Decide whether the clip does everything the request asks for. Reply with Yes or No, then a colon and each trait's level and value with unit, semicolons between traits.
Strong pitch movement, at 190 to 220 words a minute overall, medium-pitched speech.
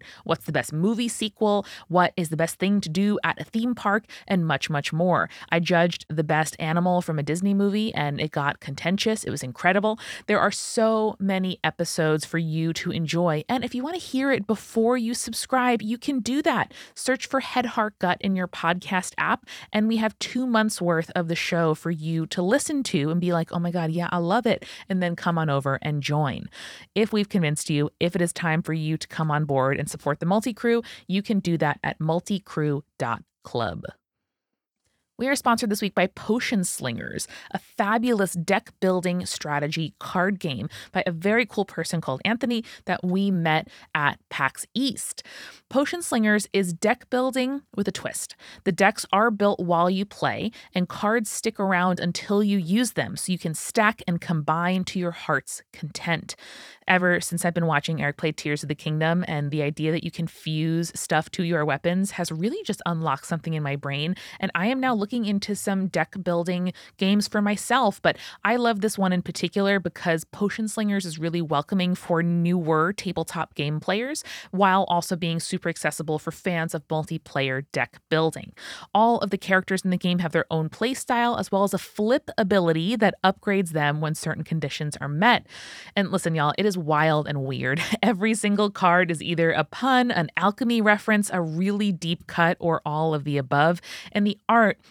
No: average, 4.5 semitones; average, 195 wpm; medium, 180 Hz